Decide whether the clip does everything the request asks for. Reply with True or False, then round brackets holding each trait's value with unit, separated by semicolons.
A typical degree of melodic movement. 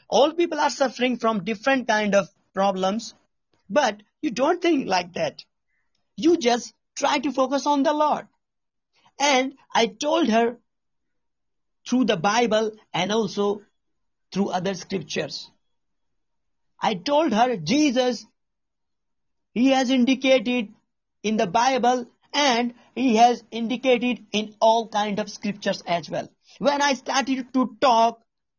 True (3.8 semitones)